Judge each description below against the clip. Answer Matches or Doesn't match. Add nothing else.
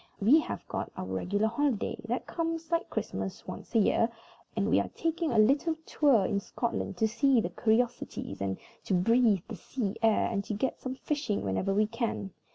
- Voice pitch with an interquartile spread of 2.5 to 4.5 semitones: Doesn't match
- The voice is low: Doesn't match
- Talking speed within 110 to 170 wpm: Doesn't match